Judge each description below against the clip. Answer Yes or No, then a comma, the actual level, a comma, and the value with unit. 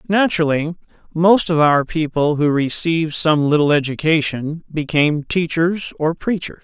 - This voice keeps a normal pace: No, slow, 125 wpm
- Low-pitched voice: No, medium, 160 Hz